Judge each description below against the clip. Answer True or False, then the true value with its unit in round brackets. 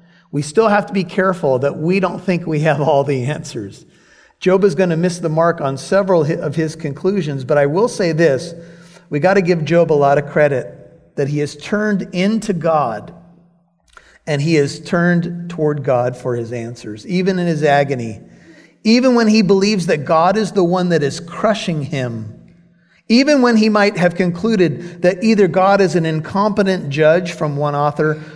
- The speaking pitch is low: False (170 Hz)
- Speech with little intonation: False (4.1 semitones)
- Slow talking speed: False (190 wpm)